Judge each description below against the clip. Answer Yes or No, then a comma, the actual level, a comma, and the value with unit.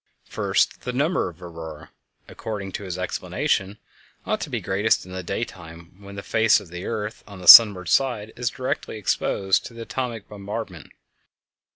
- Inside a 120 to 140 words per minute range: No, average, 170 wpm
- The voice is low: Yes, low, 100 Hz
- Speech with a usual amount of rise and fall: Yes, average, 3.6 semitones